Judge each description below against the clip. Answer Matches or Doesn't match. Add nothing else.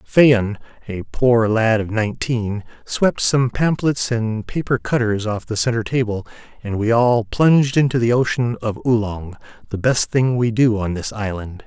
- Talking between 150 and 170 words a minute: Matches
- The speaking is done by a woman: Doesn't match